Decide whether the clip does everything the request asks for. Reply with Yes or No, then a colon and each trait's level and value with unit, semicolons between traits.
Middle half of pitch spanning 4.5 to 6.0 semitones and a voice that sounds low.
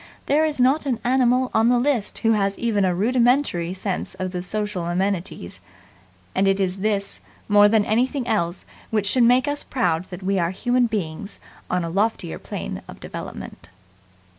No: average, 4.8 semitones; high, 210 Hz